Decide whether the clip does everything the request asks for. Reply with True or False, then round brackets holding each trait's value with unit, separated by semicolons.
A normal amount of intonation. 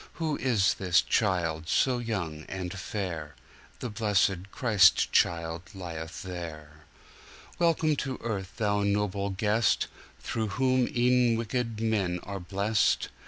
True (4.5 semitones)